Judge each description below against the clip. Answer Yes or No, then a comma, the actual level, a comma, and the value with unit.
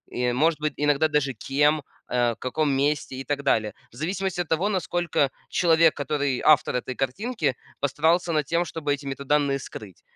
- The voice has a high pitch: No, medium, 145 Hz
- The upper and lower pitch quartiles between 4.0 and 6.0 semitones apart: No, average, 3.1 semitones